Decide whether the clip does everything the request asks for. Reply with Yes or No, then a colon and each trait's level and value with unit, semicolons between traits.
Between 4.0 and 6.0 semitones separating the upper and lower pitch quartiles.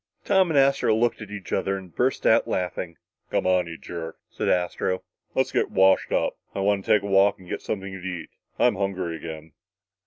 No: average, 2.7 semitones